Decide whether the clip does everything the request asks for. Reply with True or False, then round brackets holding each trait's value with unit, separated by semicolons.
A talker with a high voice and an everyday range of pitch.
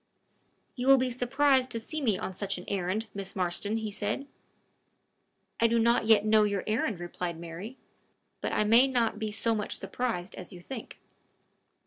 True (220 Hz; 3.6 semitones)